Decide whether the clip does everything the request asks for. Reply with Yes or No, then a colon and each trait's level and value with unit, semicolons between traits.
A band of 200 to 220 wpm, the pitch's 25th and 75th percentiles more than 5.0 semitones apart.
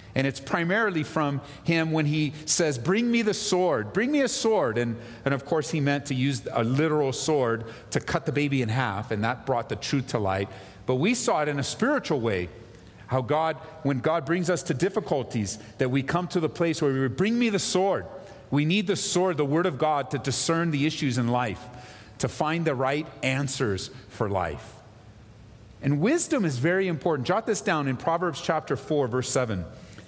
Yes: fast, 205 wpm; wide, 5.4 semitones